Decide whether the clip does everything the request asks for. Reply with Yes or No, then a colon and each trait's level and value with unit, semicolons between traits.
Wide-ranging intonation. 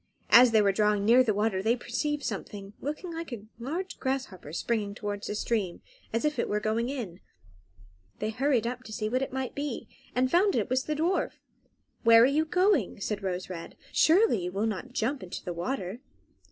No: average, 4.8 semitones